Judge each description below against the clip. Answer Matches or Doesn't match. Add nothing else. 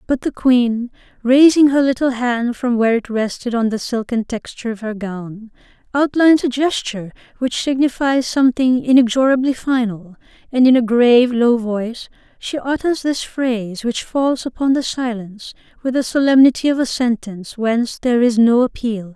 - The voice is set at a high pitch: Matches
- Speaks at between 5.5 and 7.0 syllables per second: Doesn't match